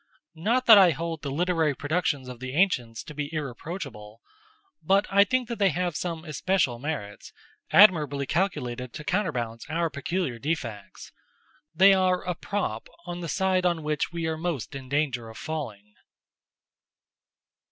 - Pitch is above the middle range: No, medium, 160 Hz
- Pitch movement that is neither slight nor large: No, wide, 5.7 semitones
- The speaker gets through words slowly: No, average, 150 wpm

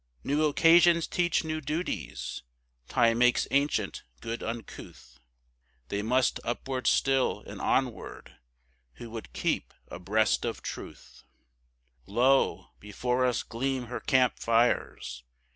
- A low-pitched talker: Yes, low, 125 Hz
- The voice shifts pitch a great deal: No, average, 3.5 semitones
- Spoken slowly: Yes, slow, 110 wpm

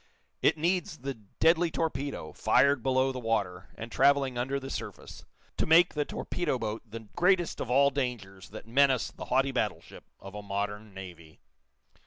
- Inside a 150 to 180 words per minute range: Yes, average, 165 wpm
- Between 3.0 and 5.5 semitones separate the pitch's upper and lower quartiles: Yes, average, 4.8 semitones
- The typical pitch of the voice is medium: No, low, 130 Hz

